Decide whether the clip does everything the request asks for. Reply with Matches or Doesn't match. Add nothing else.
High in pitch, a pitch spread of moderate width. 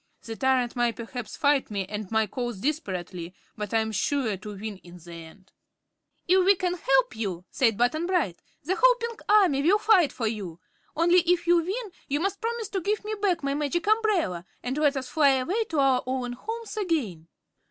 Doesn't match